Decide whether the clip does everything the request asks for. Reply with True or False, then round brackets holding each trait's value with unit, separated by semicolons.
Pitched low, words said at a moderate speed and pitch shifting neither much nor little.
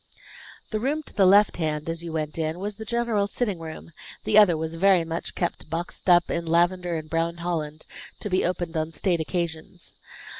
False (170 Hz; 195 wpm; 3.1 semitones)